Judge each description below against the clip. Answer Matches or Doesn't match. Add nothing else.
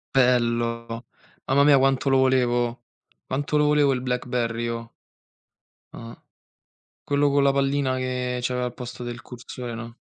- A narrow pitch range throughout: Matches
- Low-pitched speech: Matches